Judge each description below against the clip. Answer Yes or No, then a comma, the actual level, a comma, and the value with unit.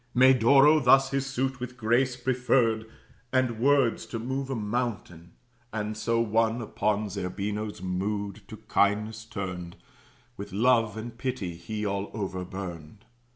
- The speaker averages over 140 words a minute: No, slow, 135 wpm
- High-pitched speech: No, low, 110 Hz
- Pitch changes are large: No, average, 3.8 semitones